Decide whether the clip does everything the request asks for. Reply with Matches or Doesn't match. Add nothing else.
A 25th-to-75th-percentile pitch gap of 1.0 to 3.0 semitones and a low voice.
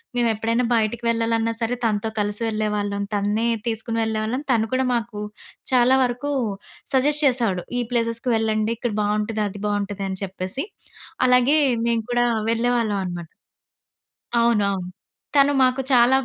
Doesn't match